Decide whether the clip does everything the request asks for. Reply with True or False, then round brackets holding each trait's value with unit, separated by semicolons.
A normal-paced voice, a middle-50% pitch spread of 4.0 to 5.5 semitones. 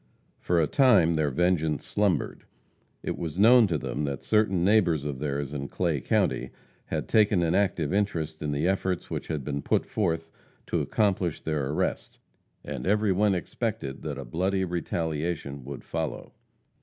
True (165 wpm; 4.6 semitones)